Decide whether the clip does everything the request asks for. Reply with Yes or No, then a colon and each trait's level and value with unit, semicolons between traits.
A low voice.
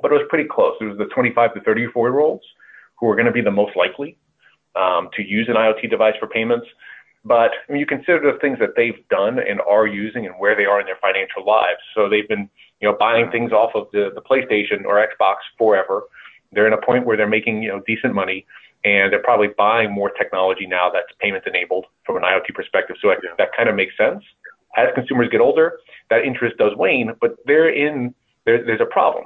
Yes: low, 120 Hz